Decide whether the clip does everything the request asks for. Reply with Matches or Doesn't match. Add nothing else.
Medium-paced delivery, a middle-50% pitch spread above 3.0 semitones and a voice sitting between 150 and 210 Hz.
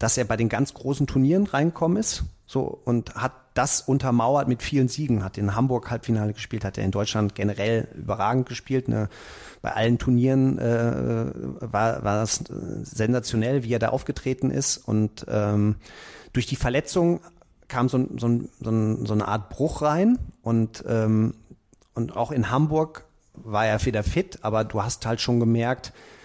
Doesn't match